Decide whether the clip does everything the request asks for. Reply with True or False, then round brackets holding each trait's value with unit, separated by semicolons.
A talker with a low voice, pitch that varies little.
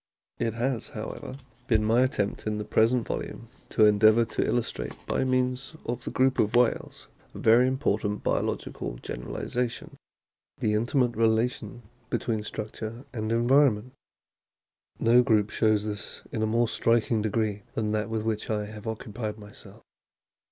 True (110 Hz; 2.2 semitones)